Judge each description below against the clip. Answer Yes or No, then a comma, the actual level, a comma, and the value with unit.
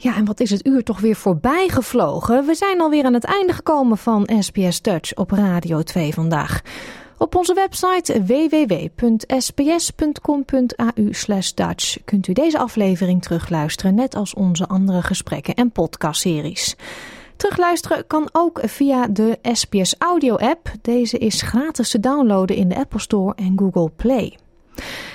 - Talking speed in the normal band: Yes, average, 145 wpm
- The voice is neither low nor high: No, high, 230 Hz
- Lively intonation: Yes, wide, 6.1 semitones